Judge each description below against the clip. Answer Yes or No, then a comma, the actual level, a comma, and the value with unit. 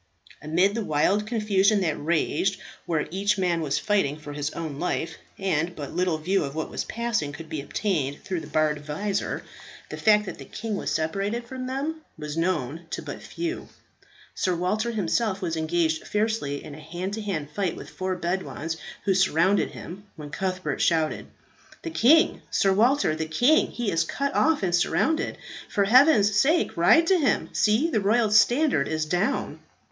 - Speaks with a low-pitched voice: No, high, 190 Hz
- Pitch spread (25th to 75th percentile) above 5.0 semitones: Yes, wide, 5.4 semitones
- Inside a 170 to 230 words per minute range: Yes, average, 180 wpm